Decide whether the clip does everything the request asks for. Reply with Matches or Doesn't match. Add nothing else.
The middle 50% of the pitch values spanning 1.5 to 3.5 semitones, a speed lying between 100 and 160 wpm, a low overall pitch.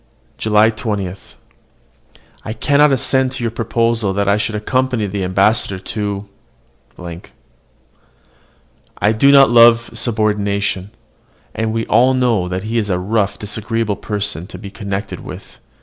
Matches